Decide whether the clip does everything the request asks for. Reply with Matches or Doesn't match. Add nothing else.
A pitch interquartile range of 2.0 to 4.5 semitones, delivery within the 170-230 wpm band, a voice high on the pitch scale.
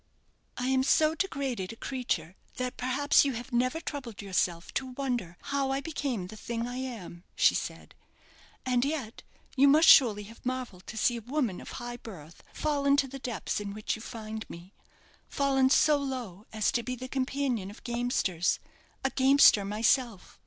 Matches